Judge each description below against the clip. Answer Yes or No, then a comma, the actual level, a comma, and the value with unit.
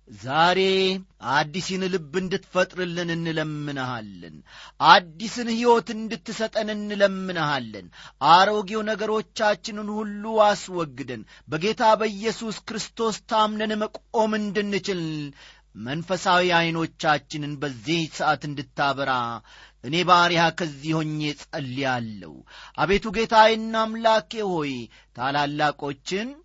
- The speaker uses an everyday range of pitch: No, wide, 6.4 semitones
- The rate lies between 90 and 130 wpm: No, average, 75 wpm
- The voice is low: No, medium, 180 Hz